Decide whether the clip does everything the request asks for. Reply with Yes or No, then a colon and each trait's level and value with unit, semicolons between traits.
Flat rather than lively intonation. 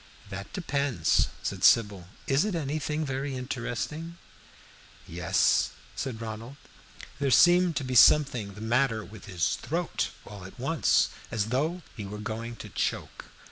No: average, 5.3 semitones